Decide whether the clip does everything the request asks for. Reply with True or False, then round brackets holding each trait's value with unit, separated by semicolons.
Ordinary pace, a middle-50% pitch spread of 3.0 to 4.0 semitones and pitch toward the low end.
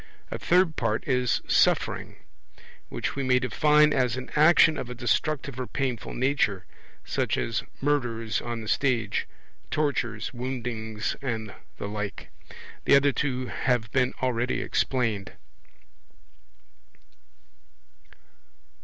False (115 wpm; 3.3 semitones; 125 Hz)